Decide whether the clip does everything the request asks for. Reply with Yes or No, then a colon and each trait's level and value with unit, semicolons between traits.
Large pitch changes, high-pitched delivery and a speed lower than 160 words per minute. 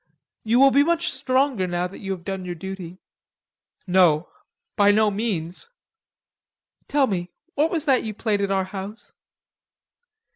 Yes: wide, 5.7 semitones; high, 200 Hz; average, 150 wpm